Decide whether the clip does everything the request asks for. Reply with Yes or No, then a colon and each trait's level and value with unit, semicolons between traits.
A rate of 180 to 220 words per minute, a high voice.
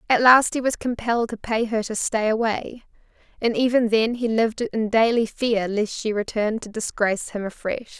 Yes: average, 195 wpm; high, 225 Hz